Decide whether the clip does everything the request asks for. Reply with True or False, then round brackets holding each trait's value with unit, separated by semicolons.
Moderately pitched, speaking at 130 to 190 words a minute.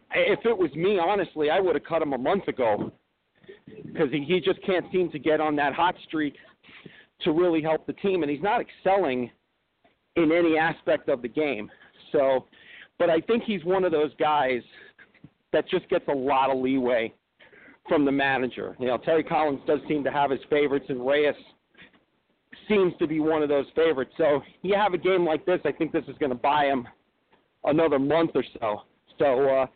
False (155 Hz; 200 wpm)